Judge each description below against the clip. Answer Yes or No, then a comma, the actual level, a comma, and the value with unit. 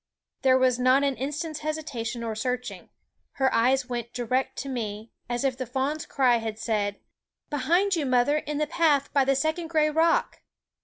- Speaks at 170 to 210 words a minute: Yes, average, 185 wpm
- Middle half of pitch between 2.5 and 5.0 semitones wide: Yes, average, 3.7 semitones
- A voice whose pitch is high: Yes, very high, 265 Hz